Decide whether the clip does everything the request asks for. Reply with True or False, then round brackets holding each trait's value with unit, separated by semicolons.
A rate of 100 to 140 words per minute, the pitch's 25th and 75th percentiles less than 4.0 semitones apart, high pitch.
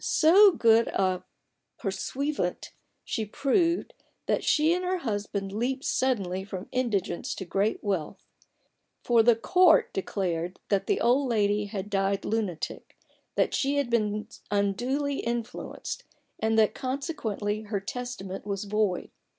False (135 wpm; 4.8 semitones; 215 Hz)